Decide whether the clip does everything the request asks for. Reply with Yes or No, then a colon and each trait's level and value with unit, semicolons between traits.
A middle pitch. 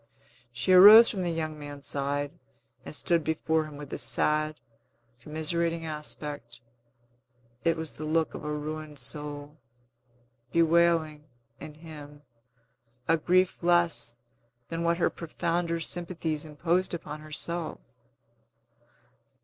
Yes: medium, 155 Hz